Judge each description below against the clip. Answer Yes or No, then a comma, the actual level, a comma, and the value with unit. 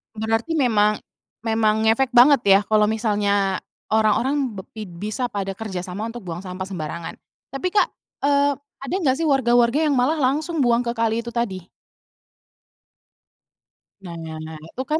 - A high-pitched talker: Yes, high, 225 Hz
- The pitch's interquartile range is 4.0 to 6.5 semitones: Yes, average, 4.7 semitones